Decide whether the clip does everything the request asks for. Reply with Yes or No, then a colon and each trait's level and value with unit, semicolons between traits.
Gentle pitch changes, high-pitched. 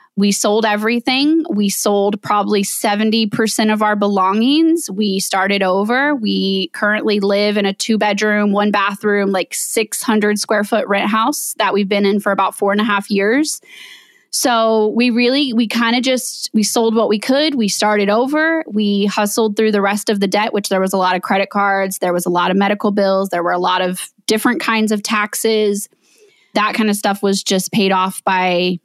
Yes: narrow, 2.2 semitones; high, 210 Hz